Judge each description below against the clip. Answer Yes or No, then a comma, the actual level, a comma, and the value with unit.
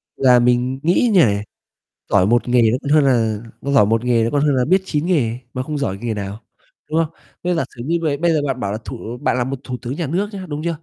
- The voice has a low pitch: Yes, low, 130 Hz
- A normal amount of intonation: Yes, average, 4.7 semitones